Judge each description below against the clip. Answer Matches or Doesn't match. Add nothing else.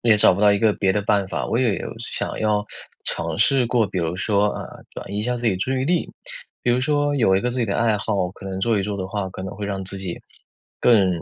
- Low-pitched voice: Matches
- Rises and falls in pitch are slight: Doesn't match